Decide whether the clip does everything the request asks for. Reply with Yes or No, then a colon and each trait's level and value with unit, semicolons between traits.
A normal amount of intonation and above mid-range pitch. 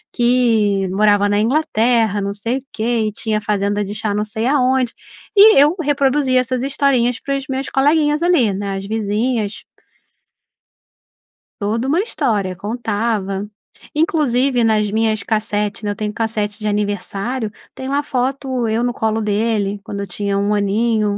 Yes: average, 3.8 semitones; high, 220 Hz